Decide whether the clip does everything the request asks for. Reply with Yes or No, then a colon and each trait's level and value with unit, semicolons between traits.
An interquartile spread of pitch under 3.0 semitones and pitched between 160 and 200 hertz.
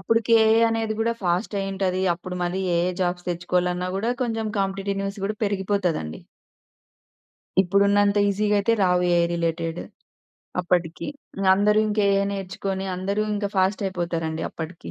Yes: narrow, 2.4 semitones; high, 195 Hz